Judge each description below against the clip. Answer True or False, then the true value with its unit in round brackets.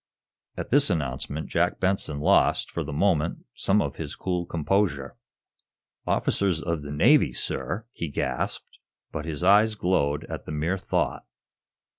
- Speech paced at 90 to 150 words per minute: True (145 wpm)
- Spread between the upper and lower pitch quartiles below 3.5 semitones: False (4.8 semitones)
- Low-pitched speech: True (80 Hz)